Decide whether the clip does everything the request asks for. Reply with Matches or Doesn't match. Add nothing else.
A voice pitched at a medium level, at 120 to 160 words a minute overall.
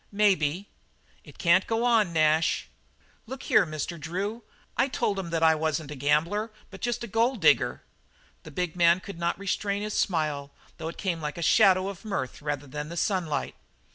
Doesn't match